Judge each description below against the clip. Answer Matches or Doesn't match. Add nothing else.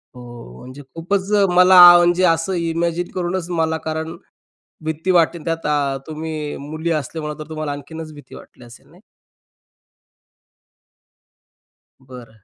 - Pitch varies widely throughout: Doesn't match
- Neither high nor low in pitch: Matches